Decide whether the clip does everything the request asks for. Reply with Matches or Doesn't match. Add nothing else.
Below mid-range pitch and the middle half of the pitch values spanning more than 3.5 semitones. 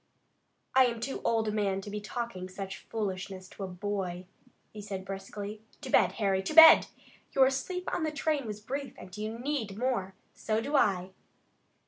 Doesn't match